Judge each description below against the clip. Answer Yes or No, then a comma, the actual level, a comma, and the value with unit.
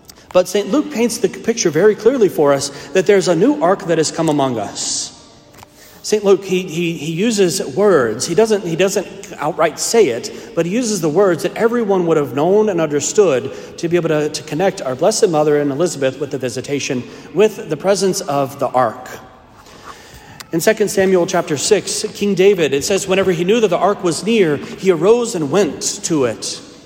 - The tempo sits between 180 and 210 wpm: Yes, average, 200 wpm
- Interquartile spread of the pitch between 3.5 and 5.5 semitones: Yes, average, 5.0 semitones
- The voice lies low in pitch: No, medium, 185 Hz